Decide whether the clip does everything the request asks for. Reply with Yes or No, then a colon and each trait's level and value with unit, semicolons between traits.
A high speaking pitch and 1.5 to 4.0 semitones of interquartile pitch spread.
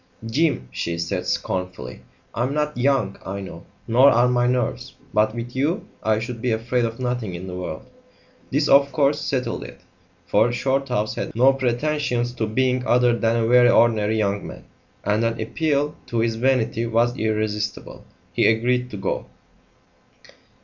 No: low, 120 Hz; average, 2.9 semitones